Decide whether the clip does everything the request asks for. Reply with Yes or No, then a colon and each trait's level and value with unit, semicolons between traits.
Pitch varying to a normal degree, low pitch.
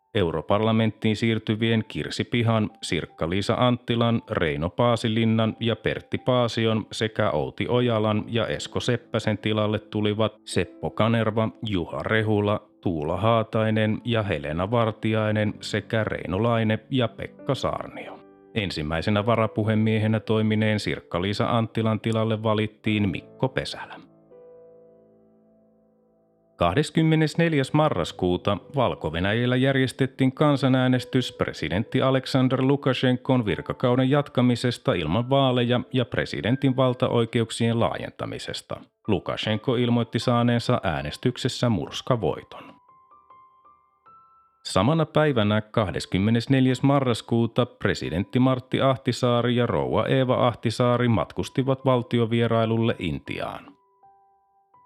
Yes: average, 3.3 semitones; low, 115 Hz